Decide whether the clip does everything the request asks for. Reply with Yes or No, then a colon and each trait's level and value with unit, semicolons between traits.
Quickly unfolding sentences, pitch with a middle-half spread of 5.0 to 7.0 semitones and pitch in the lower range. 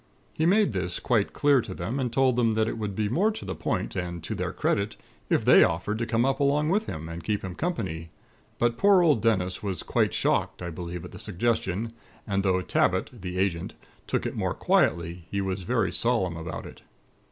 Yes: fast, 215 wpm; average, 5.3 semitones; low, 100 Hz